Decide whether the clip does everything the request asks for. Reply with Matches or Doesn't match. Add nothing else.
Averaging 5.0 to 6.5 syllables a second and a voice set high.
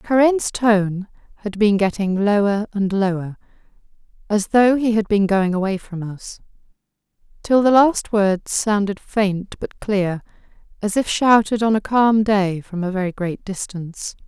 Doesn't match